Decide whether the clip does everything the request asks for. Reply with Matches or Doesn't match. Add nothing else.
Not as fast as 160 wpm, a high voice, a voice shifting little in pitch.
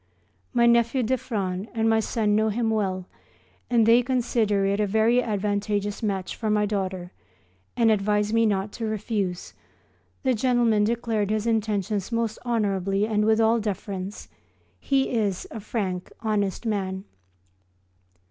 Matches